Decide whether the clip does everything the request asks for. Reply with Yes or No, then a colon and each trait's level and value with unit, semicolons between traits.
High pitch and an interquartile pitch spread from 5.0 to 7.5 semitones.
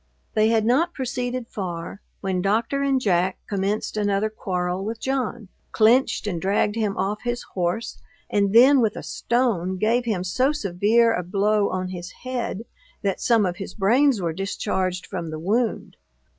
No: high, 210 Hz; average, 4.1 semitones